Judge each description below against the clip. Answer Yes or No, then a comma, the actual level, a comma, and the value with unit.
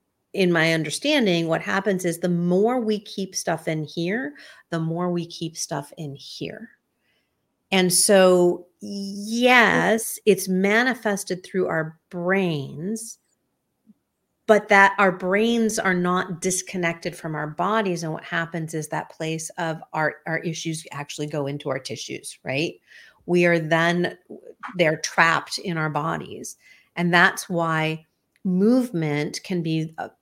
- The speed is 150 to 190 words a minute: No, slow, 135 wpm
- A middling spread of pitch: Yes, average, 3.7 semitones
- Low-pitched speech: No, medium, 175 Hz